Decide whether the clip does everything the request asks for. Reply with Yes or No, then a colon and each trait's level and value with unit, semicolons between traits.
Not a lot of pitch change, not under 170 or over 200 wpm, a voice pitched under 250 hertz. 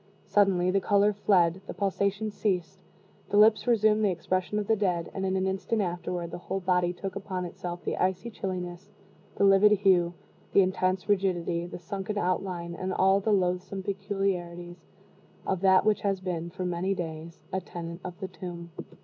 Yes: narrow, 2.1 semitones; average, 175 wpm; medium, 185 Hz